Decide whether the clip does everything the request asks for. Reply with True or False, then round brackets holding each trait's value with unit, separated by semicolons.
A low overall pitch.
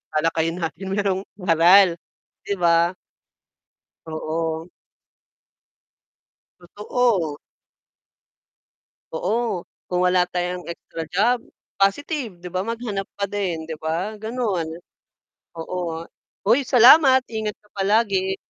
False (190 Hz)